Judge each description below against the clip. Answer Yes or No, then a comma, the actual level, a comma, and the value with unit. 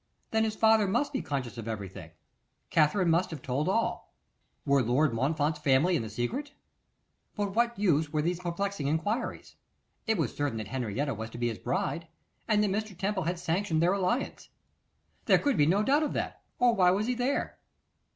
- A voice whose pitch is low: No, medium, 170 Hz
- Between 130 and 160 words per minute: No, average, 190 wpm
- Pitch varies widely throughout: Yes, wide, 7.1 semitones